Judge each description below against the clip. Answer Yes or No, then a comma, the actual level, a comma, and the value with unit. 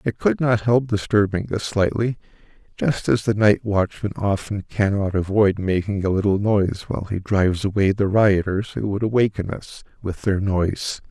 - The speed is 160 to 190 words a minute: Yes, average, 175 wpm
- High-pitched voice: No, low, 100 Hz